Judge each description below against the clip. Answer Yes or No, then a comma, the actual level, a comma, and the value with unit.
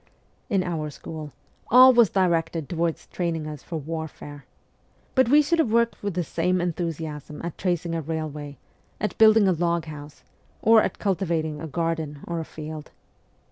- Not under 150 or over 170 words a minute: Yes, average, 165 wpm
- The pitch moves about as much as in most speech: Yes, average, 3.2 semitones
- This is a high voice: No, medium, 165 Hz